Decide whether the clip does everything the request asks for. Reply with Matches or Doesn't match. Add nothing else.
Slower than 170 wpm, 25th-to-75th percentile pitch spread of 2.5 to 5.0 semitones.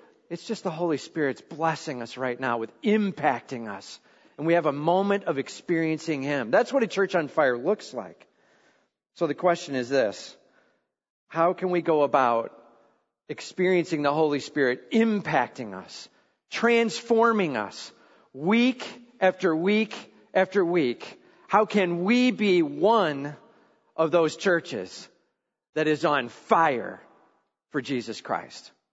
Doesn't match